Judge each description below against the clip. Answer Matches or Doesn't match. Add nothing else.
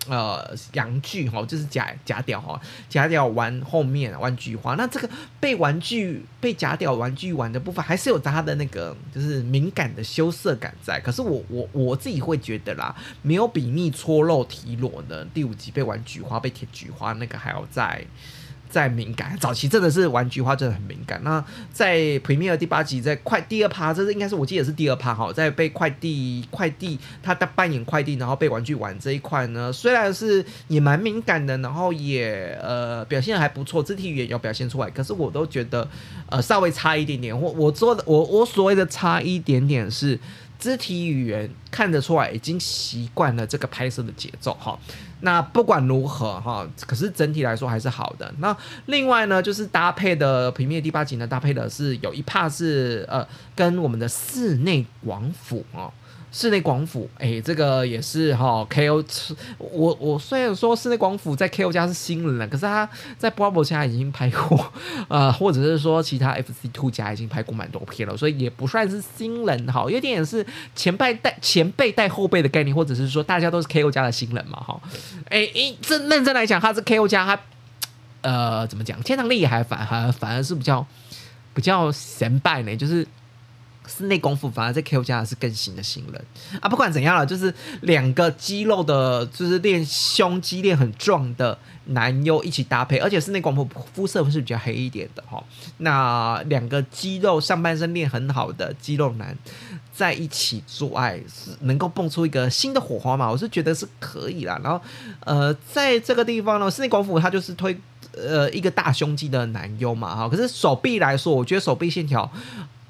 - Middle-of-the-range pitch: Matches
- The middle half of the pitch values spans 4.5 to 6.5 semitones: Matches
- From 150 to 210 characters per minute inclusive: Doesn't match